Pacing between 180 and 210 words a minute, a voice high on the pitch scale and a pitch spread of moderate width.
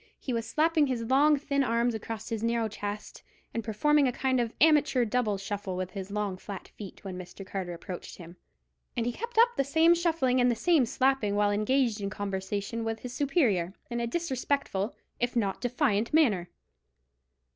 Yes: average, 185 wpm; high, 230 Hz; average, 5.0 semitones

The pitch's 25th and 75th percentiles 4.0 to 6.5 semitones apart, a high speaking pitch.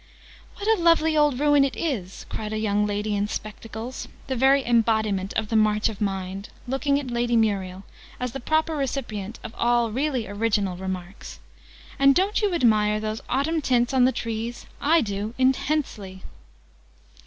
Yes: average, 4.7 semitones; high, 230 Hz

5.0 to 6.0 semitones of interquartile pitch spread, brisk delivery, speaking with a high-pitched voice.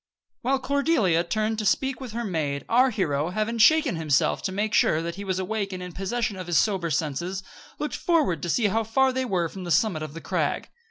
Yes: wide, 5.5 semitones; fast, 225 wpm; high, 200 Hz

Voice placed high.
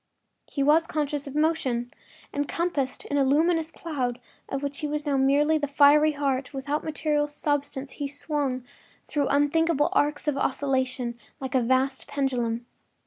Yes: very high, 285 Hz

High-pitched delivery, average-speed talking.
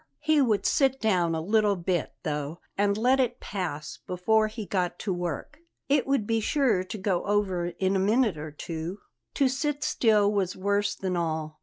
Yes: high, 200 Hz; average, 185 wpm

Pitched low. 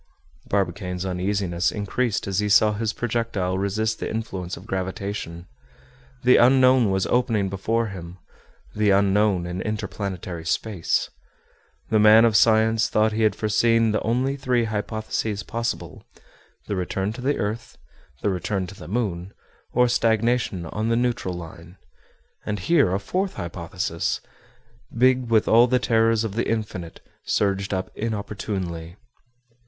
Yes: low, 105 Hz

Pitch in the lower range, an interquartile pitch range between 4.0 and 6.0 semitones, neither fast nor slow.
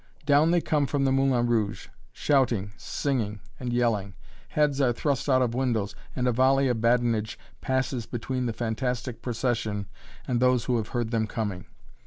No: low, 120 Hz; average, 2.8 semitones; average, 170 wpm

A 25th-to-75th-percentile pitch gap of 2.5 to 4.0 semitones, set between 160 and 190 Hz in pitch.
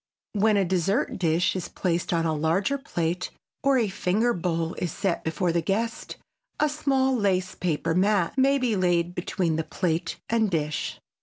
No: average, 4.6 semitones; medium, 185 Hz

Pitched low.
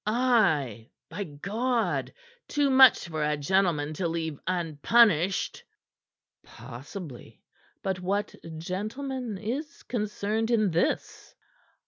No: high, 190 Hz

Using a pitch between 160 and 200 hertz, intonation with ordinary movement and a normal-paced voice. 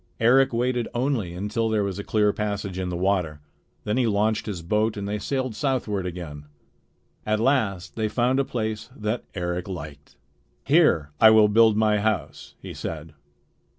No: low, 105 Hz; average, 3.6 semitones; average, 170 wpm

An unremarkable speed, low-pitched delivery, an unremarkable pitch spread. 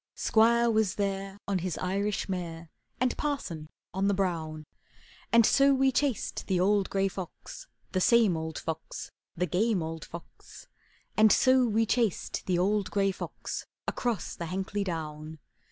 No: average, 155 wpm; high, 195 Hz; average, 4.5 semitones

